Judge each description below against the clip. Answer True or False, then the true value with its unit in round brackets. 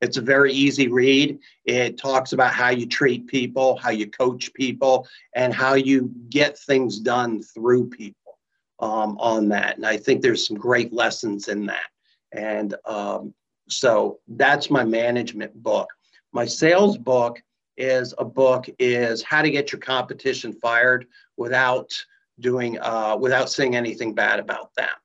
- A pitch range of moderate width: False (2.3 semitones)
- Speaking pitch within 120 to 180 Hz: True (125 Hz)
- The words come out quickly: False (155 wpm)